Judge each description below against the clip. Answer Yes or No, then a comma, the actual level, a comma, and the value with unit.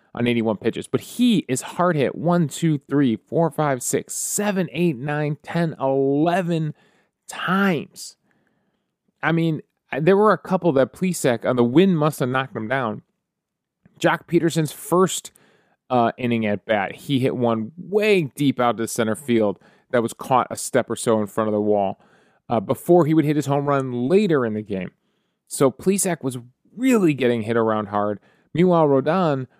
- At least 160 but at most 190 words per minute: Yes, average, 175 wpm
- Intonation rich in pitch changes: Yes, wide, 6.5 semitones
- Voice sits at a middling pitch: Yes, medium, 150 Hz